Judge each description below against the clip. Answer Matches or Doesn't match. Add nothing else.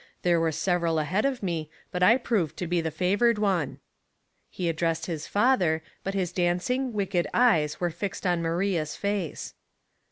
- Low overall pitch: Doesn't match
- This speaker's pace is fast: Doesn't match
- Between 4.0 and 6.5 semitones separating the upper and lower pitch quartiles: Doesn't match